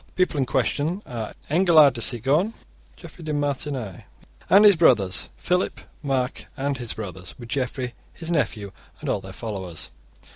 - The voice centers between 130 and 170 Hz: Yes, low, 135 Hz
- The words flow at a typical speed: Yes, average, 155 wpm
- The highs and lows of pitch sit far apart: Yes, wide, 5.9 semitones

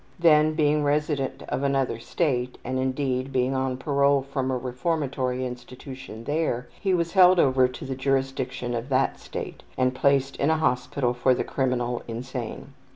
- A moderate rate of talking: Yes, average, 160 wpm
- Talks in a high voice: No, low, 130 Hz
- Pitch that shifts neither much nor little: No, narrow, 2.0 semitones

